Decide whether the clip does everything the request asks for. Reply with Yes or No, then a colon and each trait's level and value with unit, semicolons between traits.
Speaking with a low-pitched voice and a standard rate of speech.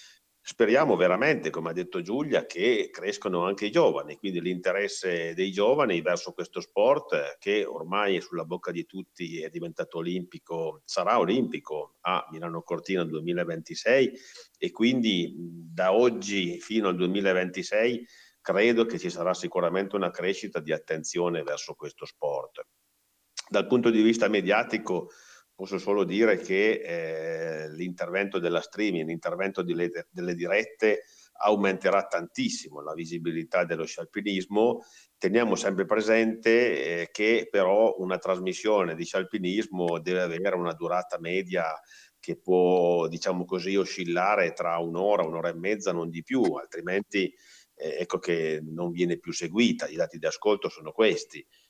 Yes: very low, 95 Hz; average, 140 wpm